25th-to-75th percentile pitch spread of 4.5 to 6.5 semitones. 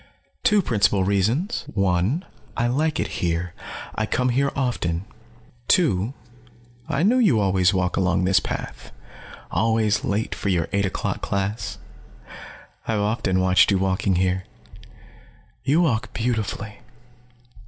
Yes: average, 5.1 semitones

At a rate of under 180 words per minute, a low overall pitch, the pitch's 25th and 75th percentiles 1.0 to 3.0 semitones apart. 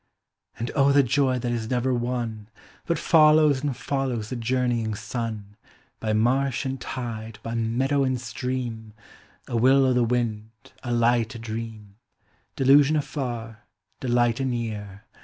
Yes: average, 140 wpm; low, 120 Hz; average, 2.7 semitones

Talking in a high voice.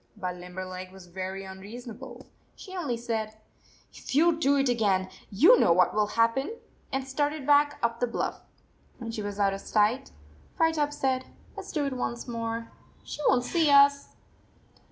Yes: high, 235 Hz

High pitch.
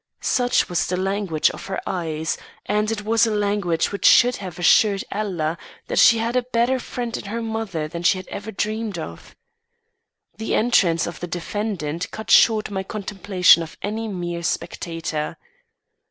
Yes: high, 200 Hz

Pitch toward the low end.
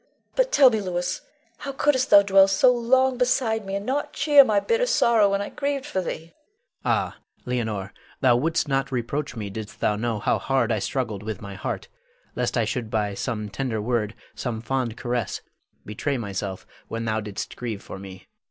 Yes: low, 130 Hz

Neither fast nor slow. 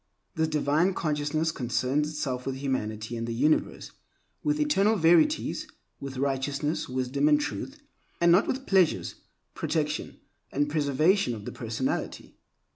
No: slow, 130 wpm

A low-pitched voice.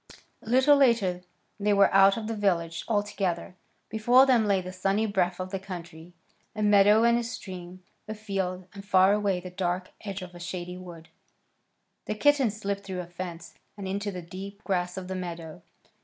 No: high, 195 Hz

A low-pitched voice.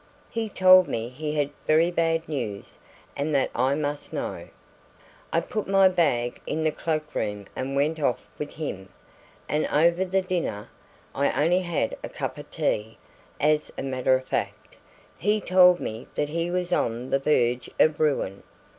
No: medium, 150 Hz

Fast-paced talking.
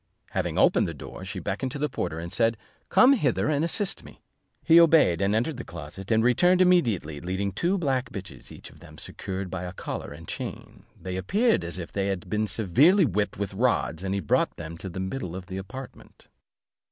Yes: fast, 210 wpm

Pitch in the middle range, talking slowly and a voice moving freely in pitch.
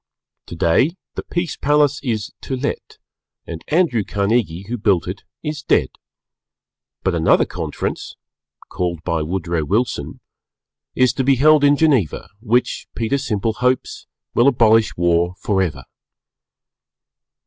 No: low, 115 Hz; slow, 125 wpm; wide, 7.5 semitones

